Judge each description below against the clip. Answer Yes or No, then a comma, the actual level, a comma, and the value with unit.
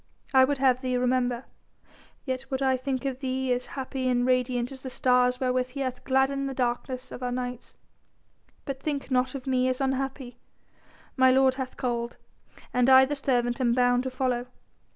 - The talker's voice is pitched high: Yes, very high, 255 Hz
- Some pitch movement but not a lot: No, narrow, 1.1 semitones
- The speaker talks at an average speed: Yes, average, 185 wpm